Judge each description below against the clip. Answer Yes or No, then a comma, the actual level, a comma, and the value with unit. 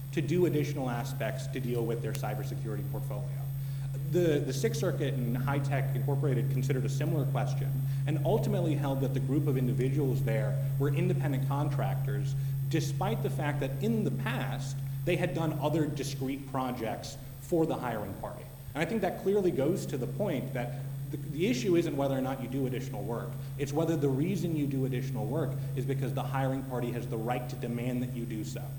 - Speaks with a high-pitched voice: No, low, 135 Hz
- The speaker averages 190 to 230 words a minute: Yes, average, 195 wpm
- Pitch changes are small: Yes, narrow, 1.3 semitones